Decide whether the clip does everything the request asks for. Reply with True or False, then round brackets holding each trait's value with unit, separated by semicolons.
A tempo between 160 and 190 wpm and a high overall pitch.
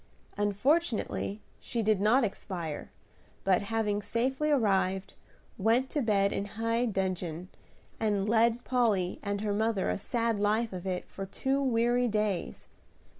False (135 wpm; 215 Hz)